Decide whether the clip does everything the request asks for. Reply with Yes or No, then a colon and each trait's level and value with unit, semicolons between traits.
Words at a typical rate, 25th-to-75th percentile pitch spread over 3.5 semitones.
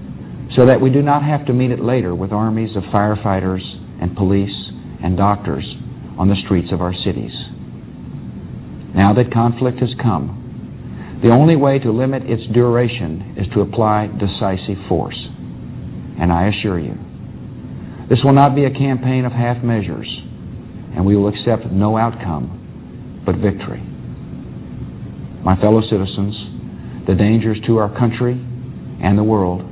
Yes: average, 145 wpm; average, 4.3 semitones